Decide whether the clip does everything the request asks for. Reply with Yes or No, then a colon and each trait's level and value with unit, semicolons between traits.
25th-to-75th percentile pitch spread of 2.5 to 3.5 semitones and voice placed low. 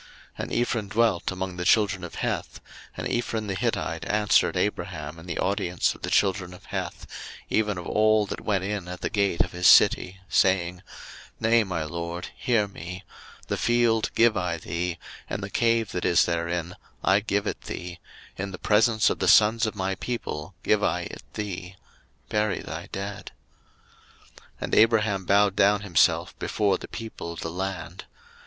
Yes: average, 3.1 semitones; very low, 95 Hz